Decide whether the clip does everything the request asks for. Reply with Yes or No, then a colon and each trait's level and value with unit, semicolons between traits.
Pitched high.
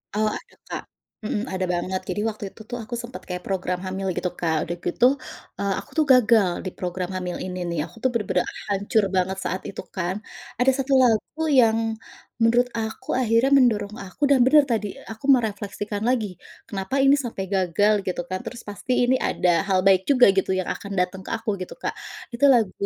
Yes: high, 205 Hz